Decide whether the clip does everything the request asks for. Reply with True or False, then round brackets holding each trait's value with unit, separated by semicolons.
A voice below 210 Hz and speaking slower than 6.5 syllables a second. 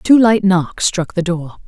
True (185 Hz; 4.0 syllables/s)